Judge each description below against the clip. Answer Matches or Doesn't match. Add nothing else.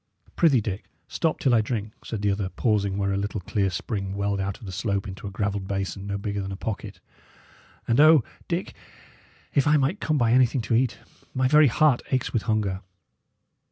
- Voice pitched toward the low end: Matches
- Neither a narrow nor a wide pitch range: Matches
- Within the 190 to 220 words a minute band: Matches